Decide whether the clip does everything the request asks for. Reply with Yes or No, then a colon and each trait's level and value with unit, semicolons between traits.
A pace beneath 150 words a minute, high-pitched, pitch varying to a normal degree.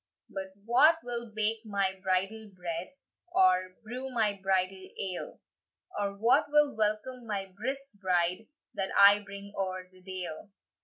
Yes: average, 140 wpm; high, 200 Hz; average, 3.1 semitones